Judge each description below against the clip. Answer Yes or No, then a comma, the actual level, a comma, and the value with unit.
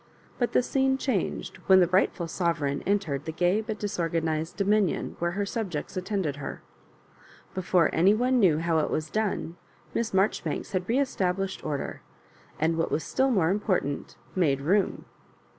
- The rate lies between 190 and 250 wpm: No, average, 165 wpm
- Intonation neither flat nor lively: Yes, average, 4.2 semitones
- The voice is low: No, medium, 185 Hz